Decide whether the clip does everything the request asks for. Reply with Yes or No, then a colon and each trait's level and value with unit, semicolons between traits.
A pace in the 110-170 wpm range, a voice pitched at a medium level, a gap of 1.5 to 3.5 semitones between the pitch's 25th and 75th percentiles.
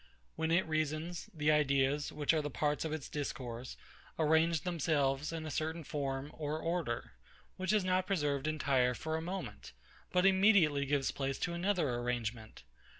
Yes: average, 160 wpm; medium, 155 Hz; average, 3.2 semitones